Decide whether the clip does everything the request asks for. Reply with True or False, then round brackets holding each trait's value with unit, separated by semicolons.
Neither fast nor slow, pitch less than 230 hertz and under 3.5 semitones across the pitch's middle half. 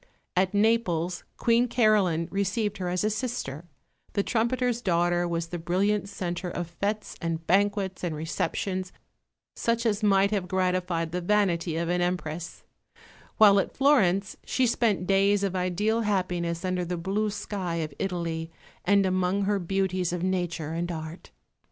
True (150 wpm; 185 Hz; 2.9 semitones)